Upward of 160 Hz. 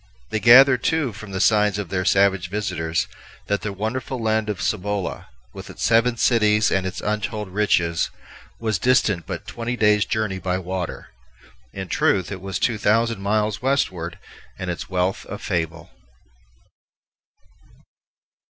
No: low, 105 Hz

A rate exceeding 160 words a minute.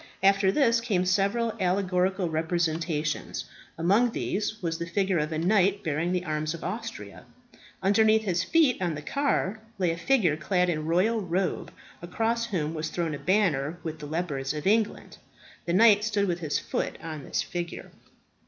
Yes: average, 170 wpm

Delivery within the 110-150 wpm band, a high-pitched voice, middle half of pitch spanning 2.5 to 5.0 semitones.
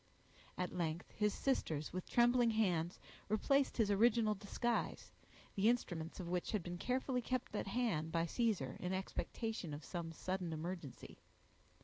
No: average, 145 wpm; high, 195 Hz; wide, 5.4 semitones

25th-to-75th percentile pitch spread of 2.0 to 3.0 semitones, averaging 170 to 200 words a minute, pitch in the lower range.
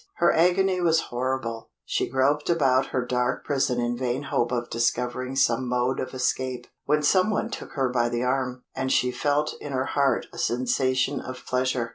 Yes: narrow, 2.4 semitones; average, 185 wpm; low, 130 Hz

